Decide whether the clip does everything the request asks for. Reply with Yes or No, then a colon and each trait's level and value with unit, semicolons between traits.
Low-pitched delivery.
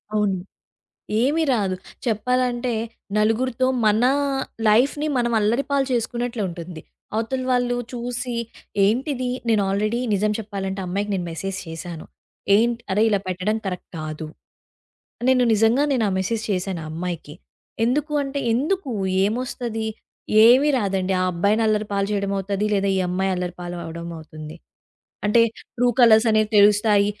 No: high, 215 Hz